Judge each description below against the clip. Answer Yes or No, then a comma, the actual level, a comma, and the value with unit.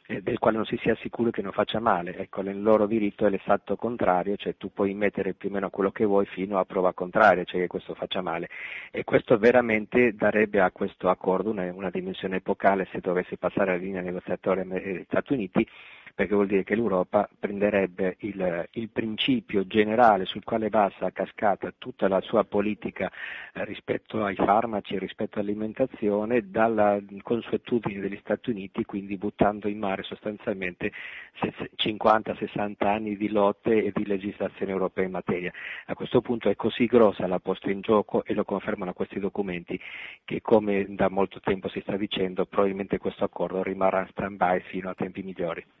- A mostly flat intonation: Yes, narrow, 2.1 semitones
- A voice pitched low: Yes, low, 100 Hz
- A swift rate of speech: Yes, fast, 175 wpm